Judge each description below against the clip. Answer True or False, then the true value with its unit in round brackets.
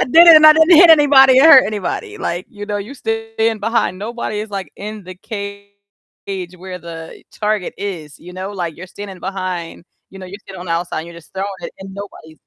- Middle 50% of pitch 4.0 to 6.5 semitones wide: False (3.4 semitones)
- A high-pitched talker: True (200 Hz)